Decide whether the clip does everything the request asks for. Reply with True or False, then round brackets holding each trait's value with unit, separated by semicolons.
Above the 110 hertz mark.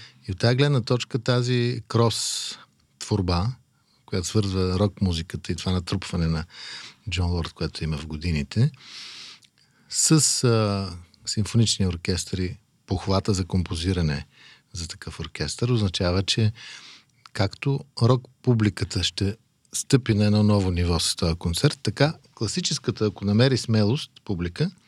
False (105 Hz)